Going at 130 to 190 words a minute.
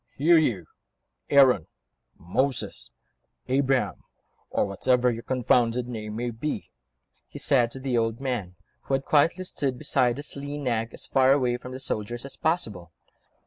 Yes: average, 150 wpm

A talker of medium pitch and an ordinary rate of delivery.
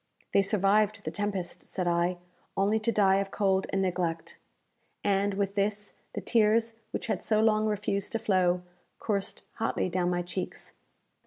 No: high, 200 Hz; average, 160 wpm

